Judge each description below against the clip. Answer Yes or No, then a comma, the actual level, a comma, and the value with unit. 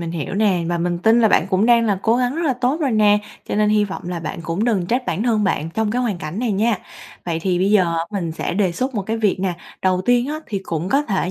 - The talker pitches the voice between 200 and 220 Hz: Yes, high, 205 Hz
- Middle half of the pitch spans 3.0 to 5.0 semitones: Yes, average, 4.6 semitones